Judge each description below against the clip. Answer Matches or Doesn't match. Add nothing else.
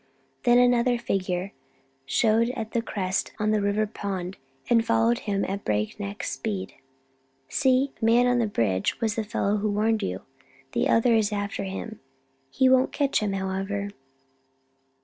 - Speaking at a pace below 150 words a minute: Doesn't match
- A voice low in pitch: Doesn't match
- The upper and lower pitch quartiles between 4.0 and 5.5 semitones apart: Doesn't match